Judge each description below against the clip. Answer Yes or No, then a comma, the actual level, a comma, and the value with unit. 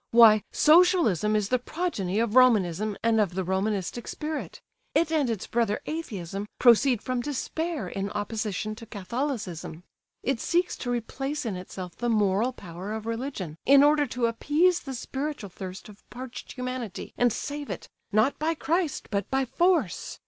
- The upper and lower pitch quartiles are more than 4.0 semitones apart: Yes, wide, 5.6 semitones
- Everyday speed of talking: Yes, average, 160 wpm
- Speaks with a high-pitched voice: Yes, high, 235 Hz